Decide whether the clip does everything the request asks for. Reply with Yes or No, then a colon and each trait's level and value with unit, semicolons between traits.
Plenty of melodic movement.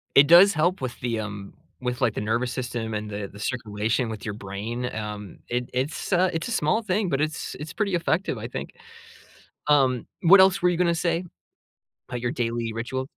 Yes: wide, 7.0 semitones